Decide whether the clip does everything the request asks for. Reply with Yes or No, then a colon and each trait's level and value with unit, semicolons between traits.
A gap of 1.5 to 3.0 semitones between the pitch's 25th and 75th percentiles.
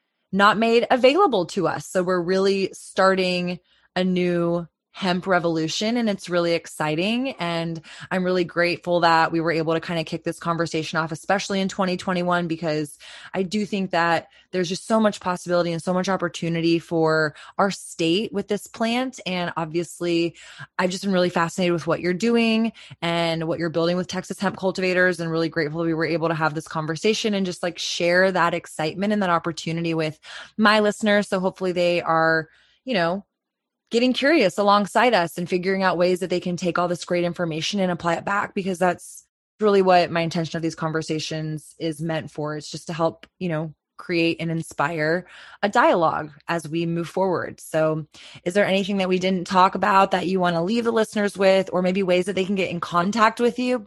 Yes: narrow, 2.6 semitones